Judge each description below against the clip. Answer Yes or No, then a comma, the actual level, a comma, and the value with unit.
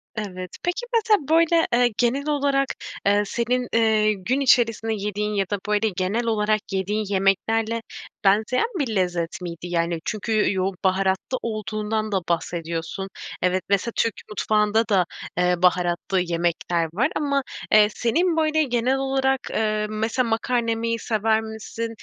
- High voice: Yes, high, 215 Hz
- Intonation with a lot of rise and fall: No, average, 3.8 semitones